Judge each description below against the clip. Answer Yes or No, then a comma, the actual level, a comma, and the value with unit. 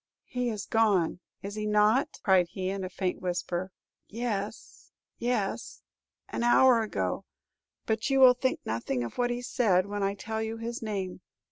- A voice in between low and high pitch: No, high, 210 Hz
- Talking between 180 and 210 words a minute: No, average, 165 wpm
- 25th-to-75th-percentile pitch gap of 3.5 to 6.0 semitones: Yes, average, 4.0 semitones